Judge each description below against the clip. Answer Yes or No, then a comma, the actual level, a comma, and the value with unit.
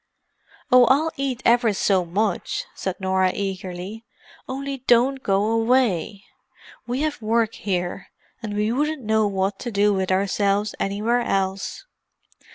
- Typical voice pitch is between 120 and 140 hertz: No, high, 210 Hz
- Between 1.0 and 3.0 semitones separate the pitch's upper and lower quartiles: No, average, 3.9 semitones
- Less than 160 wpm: Yes, slow, 135 wpm